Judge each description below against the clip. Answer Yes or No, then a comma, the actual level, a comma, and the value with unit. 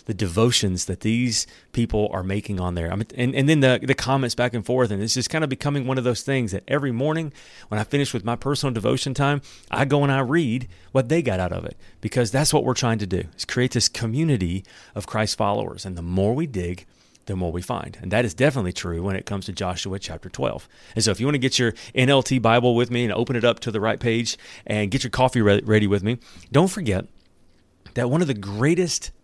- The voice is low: Yes, low, 115 Hz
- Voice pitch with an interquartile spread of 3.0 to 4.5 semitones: No, average, 5.0 semitones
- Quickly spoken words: Yes, fast, 250 wpm